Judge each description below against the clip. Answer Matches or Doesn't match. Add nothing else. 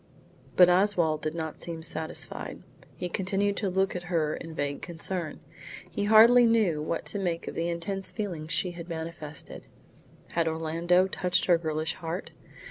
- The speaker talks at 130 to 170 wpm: Matches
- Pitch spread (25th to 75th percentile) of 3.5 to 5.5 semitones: Doesn't match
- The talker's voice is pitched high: Doesn't match